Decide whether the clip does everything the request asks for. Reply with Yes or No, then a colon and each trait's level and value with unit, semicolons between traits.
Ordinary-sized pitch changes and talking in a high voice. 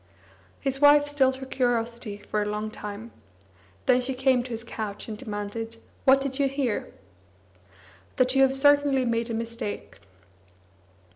Yes: average, 3.2 semitones; high, 245 Hz